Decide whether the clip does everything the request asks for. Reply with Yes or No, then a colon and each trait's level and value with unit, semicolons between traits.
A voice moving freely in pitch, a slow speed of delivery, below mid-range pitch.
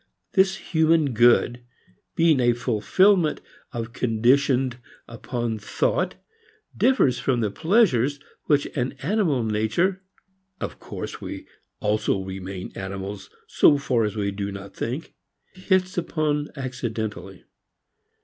Yes: wide, 6.7 semitones; slow, 110 wpm; low, 125 Hz